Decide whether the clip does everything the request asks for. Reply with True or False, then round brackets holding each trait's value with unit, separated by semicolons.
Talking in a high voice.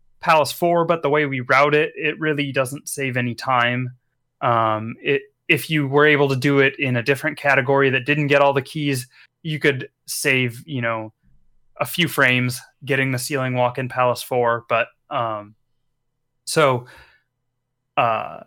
False (135 Hz)